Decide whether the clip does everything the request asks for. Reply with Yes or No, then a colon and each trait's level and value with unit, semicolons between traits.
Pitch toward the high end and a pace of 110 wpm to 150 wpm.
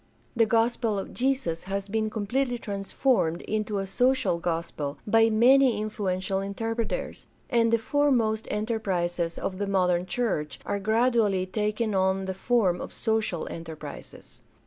Yes: high, 210 Hz; average, 140 wpm